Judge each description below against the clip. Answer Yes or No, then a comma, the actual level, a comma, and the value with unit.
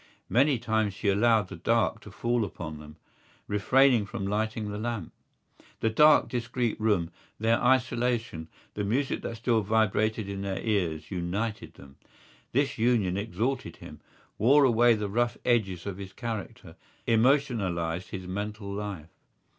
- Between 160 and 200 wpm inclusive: No, average, 145 wpm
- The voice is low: Yes, low, 110 Hz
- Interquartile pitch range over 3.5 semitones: No, average, 3.2 semitones